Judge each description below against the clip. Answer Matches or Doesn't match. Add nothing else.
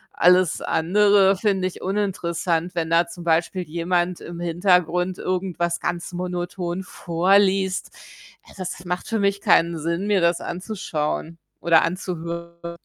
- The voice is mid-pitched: Matches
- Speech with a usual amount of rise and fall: Doesn't match